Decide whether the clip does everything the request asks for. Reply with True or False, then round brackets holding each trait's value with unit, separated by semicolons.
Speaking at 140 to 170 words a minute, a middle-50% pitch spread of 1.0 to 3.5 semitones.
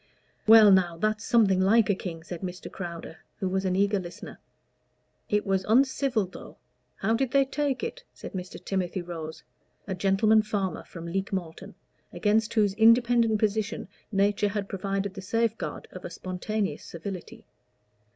True (155 wpm; 2.9 semitones)